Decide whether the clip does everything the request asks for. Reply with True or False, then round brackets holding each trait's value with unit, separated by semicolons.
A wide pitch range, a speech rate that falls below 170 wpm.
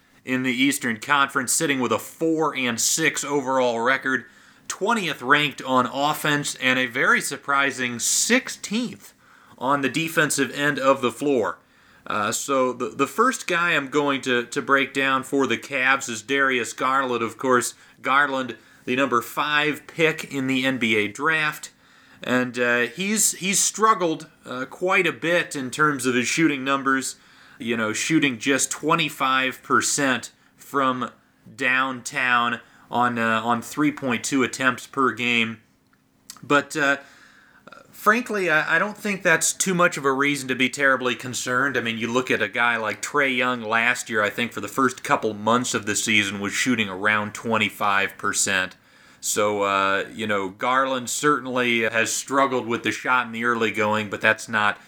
False (3.8 semitones; 160 wpm)